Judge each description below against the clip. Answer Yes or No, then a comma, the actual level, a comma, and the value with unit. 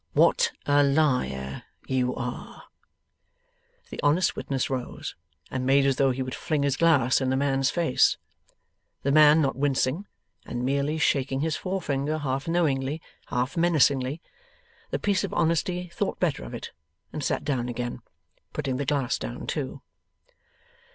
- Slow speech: No, average, 150 wpm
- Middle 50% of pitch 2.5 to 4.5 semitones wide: Yes, average, 3.0 semitones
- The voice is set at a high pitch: No, medium, 140 Hz